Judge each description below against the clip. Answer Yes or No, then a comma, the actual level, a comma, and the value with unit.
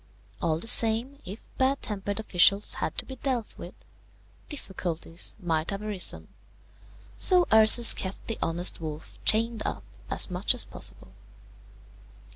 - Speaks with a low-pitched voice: No, high, 210 Hz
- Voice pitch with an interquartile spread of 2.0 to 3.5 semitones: No, average, 4.7 semitones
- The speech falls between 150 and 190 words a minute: No, slow, 135 wpm